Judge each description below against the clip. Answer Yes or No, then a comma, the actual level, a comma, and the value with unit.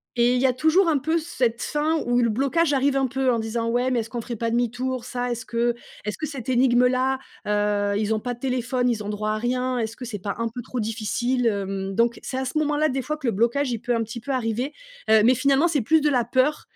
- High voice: Yes, high, 245 Hz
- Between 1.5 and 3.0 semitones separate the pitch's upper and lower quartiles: Yes, average, 2.7 semitones